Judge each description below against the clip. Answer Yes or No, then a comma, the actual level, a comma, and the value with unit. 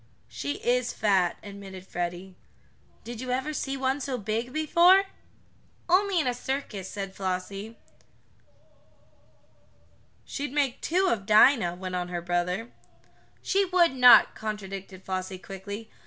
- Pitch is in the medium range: No, high, 215 Hz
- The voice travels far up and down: Yes, wide, 6.0 semitones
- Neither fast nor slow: No, slow, 130 wpm